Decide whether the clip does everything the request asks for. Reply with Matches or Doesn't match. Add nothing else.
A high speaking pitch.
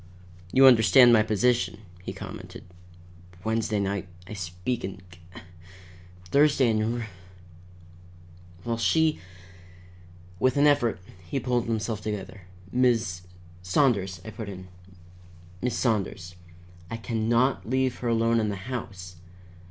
Doesn't match